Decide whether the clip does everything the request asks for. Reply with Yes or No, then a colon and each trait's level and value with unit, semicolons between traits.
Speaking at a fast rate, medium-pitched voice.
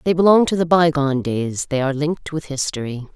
Yes: fast, 210 wpm; medium, 150 Hz